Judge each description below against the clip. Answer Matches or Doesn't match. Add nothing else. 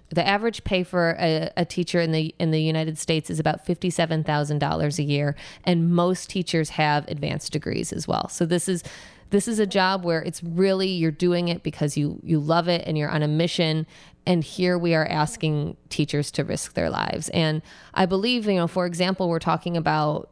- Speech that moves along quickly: Matches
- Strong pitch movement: Doesn't match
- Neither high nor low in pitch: Matches